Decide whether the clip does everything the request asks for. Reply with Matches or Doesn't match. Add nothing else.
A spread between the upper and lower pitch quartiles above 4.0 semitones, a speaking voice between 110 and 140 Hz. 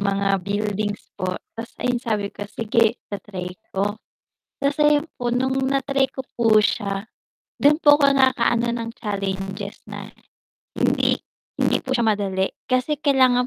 Doesn't match